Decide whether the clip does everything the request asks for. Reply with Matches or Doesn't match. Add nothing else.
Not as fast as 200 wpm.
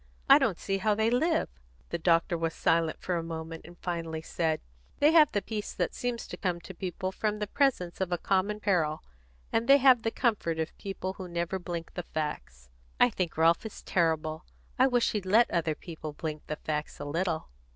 Doesn't match